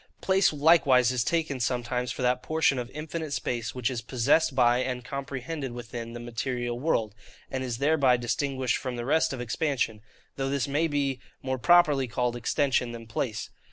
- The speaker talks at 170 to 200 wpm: Yes, average, 175 wpm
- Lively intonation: No, average, 2.9 semitones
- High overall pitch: No, low, 130 Hz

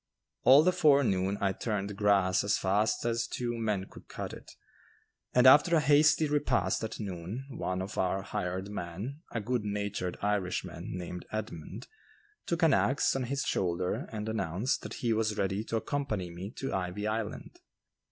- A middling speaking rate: Yes, average, 165 wpm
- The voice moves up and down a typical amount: Yes, average, 4.9 semitones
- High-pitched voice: No, low, 105 Hz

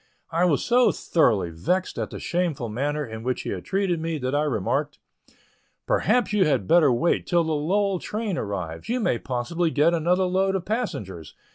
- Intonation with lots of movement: Yes, wide, 7.3 semitones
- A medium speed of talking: Yes, average, 185 wpm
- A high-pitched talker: No, medium, 160 Hz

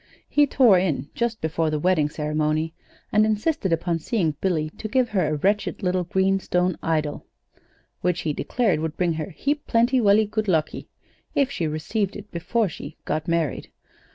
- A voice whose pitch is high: No, medium, 180 Hz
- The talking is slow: No, average, 175 wpm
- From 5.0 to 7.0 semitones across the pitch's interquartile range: Yes, wide, 5.4 semitones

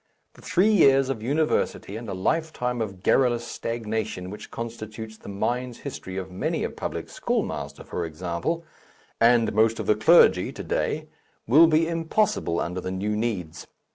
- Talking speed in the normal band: Yes, average, 160 wpm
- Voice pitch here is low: Yes, low, 115 Hz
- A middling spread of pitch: No, wide, 5.7 semitones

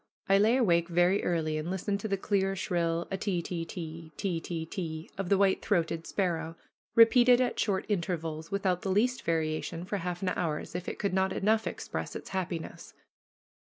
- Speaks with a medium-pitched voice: Yes, medium, 180 Hz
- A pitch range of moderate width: Yes, average, 3.1 semitones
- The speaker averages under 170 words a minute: No, average, 190 wpm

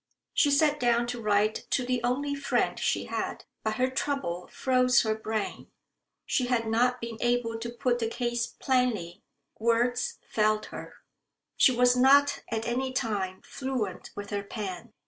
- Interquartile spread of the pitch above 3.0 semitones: No, narrow, 2.6 semitones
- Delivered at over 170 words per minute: No, average, 160 wpm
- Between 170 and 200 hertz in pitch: No, high, 240 Hz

